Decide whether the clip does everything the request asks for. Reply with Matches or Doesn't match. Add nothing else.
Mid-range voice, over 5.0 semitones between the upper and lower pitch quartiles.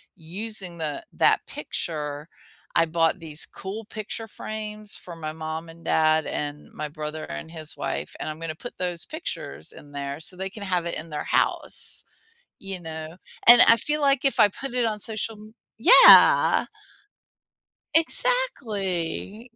Matches